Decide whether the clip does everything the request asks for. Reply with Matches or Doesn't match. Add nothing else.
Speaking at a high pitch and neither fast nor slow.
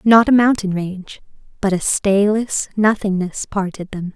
Matches